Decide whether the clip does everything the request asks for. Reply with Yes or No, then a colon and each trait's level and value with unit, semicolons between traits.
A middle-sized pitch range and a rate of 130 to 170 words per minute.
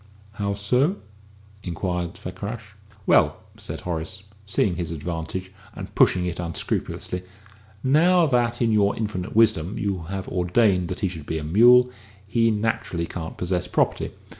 Yes: average, 4.3 semitones; average, 140 wpm